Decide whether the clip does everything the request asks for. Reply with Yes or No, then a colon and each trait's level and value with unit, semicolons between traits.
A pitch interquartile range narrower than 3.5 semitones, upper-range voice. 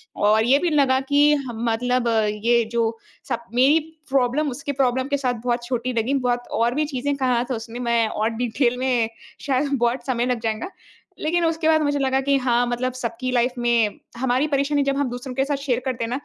Yes: narrow, 2.6 semitones; very high, 250 Hz